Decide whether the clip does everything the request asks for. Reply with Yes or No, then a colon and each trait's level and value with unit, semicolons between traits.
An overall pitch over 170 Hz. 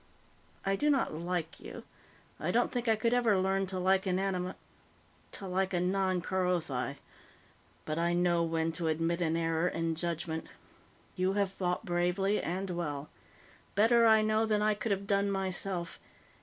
Yes: medium, 185 Hz